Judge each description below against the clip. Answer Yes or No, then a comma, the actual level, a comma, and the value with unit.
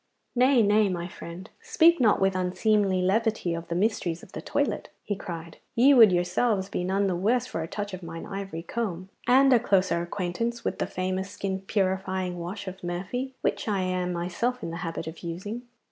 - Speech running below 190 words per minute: No, average, 195 wpm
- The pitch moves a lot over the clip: No, average, 3.8 semitones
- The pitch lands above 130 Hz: Yes, high, 190 Hz